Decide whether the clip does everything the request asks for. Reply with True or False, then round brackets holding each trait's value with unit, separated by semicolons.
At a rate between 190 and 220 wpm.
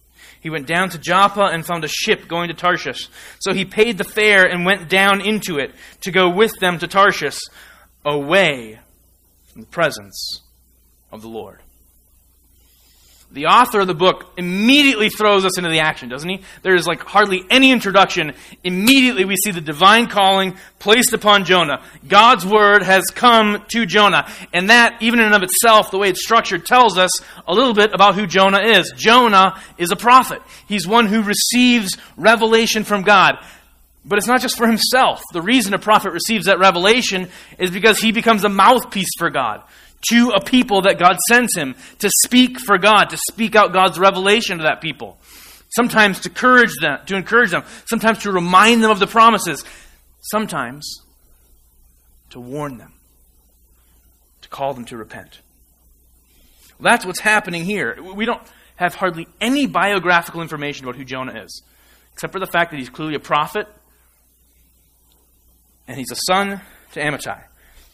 False (170 wpm)